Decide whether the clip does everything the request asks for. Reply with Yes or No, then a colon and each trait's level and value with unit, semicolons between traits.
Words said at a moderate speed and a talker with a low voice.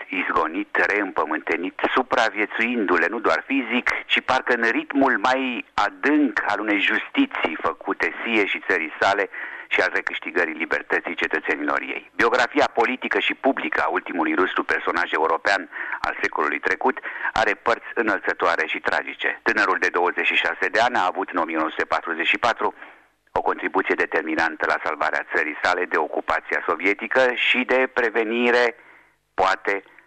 Yes: average, 130 wpm; low, 130 Hz